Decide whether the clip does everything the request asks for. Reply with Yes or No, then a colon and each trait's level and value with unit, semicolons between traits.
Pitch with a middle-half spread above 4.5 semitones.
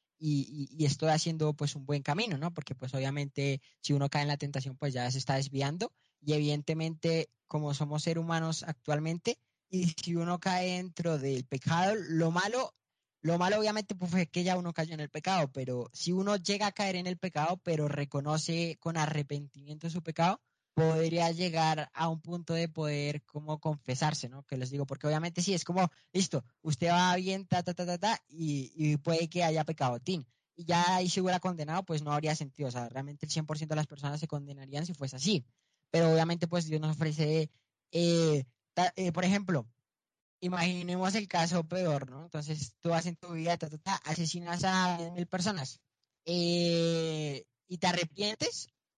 No: average, 3.2 semitones